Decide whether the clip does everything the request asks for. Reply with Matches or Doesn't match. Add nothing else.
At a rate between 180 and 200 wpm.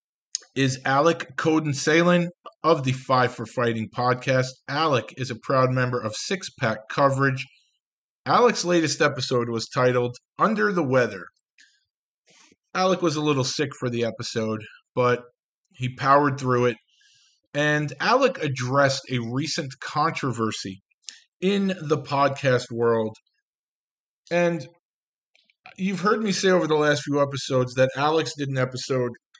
Doesn't match